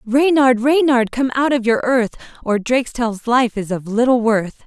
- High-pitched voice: Yes, high, 240 Hz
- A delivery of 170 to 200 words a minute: Yes, average, 180 wpm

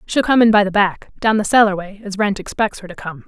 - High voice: Yes, high, 200 Hz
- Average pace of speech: No, fast, 275 wpm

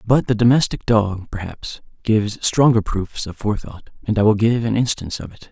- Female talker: No, male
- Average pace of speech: Yes, average, 195 wpm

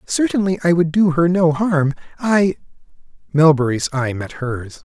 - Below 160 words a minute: Yes, slow, 135 wpm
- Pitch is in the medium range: Yes, medium, 165 Hz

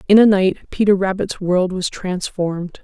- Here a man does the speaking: No, female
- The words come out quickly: No, average, 170 wpm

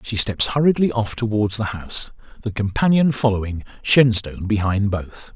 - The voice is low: Yes, low, 110 Hz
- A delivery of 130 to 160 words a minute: Yes, average, 145 wpm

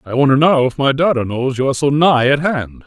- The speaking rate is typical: No, fast, 270 wpm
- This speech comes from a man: Yes, male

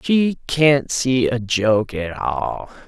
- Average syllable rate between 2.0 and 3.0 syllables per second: Yes, 2.8 syllables/s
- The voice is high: No, low, 130 Hz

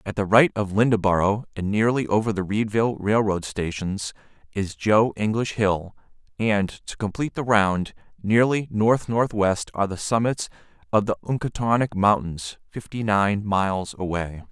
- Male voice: Yes, male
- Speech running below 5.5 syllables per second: Yes, 4.7 syllables/s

